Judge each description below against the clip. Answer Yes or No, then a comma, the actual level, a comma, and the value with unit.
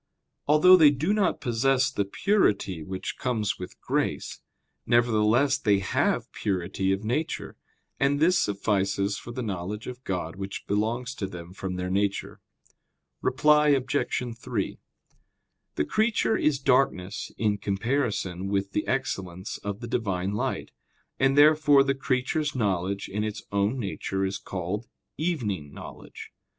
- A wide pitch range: Yes, wide, 5.7 semitones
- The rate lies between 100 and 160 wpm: Yes, average, 140 wpm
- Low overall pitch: Yes, low, 110 Hz